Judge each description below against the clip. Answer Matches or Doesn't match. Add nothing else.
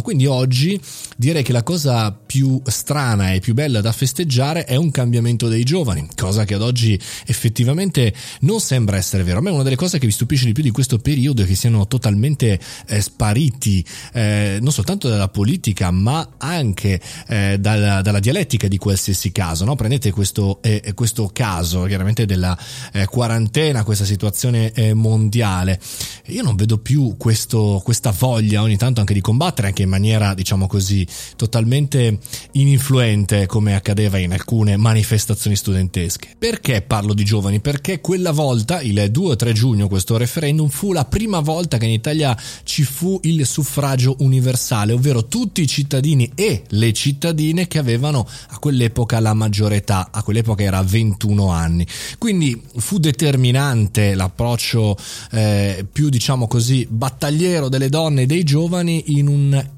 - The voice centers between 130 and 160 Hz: Doesn't match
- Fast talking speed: Doesn't match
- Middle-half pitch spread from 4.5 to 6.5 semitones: Matches